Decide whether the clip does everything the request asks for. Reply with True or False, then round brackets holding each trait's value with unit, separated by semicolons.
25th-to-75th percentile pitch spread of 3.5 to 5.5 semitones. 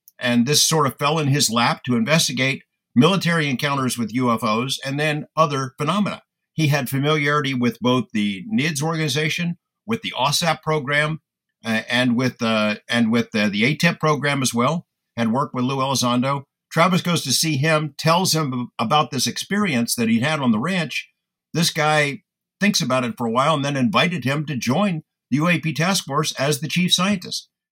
True (4.7 semitones)